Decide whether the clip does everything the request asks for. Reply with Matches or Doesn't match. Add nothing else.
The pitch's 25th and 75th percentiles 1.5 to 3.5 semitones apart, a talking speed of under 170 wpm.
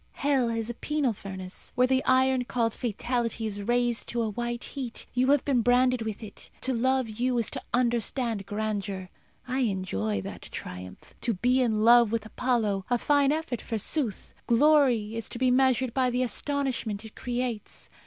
Doesn't match